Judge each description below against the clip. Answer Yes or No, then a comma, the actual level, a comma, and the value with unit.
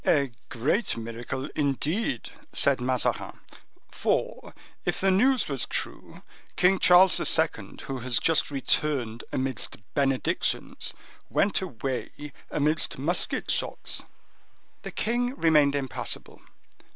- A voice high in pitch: No, medium, 140 Hz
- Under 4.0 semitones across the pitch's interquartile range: No, wide, 5.4 semitones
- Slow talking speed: Yes, slow, 105 wpm